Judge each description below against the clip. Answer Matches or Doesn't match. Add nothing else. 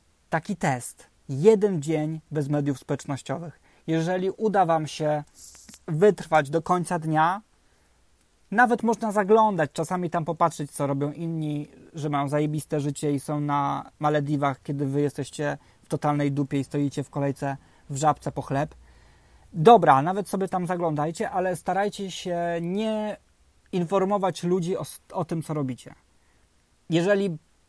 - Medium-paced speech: Matches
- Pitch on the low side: Doesn't match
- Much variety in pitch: Doesn't match